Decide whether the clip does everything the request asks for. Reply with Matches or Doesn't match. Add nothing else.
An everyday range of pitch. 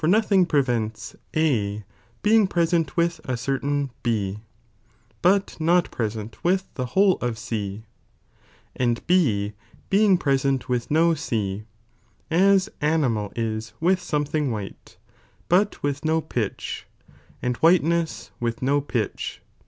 Doesn't match